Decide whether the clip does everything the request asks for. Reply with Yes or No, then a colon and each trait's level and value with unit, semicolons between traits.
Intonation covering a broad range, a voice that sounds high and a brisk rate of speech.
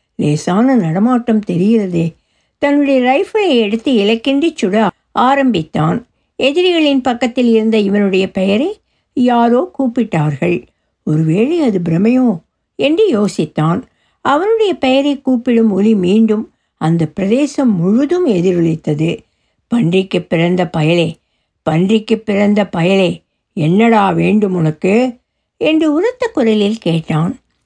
No: wide, 6.2 semitones; high, 215 Hz; average, 95 wpm